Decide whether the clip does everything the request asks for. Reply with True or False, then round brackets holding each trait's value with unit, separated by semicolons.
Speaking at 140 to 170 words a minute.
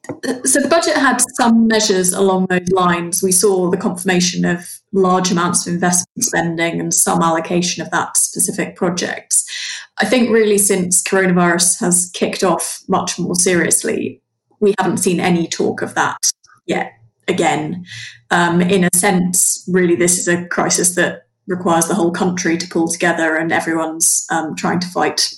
True (165 wpm)